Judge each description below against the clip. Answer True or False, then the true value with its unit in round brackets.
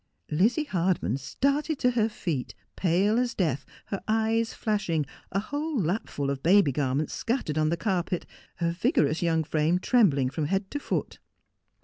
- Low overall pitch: False (185 Hz)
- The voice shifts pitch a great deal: True (6.5 semitones)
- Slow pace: False (160 wpm)